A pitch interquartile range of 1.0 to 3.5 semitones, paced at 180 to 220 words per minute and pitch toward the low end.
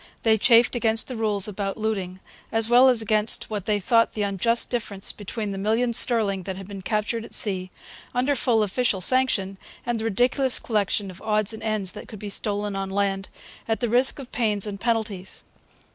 No: average, 2.8 semitones; average, 195 wpm; high, 215 Hz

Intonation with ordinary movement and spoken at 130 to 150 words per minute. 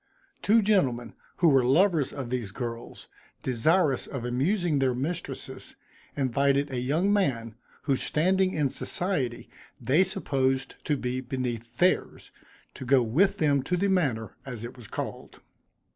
No: wide, 6.0 semitones; average, 145 wpm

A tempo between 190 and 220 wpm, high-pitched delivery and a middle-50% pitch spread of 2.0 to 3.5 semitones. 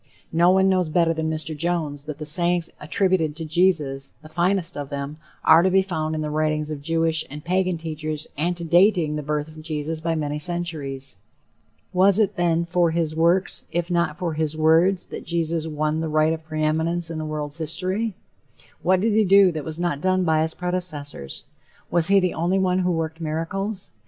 No: average, 195 wpm; medium, 165 Hz; narrow, 2.4 semitones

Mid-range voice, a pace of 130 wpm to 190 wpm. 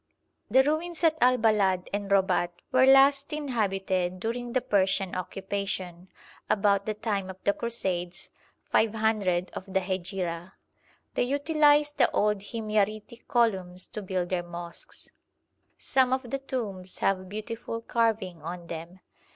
No: high, 205 Hz; slow, 135 wpm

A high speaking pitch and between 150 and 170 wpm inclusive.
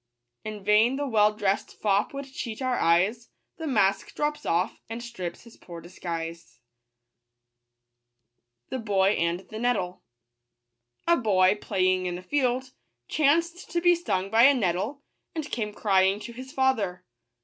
No: high, 210 Hz; average, 140 wpm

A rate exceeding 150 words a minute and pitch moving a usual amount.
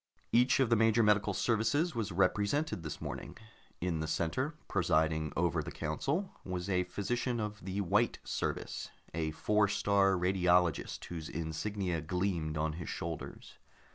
No: average, 145 wpm; average, 4.4 semitones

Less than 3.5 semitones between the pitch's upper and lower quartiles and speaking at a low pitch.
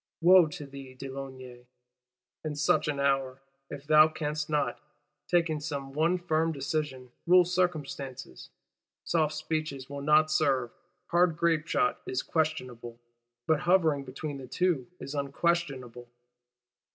No: average, 3.0 semitones; medium, 150 Hz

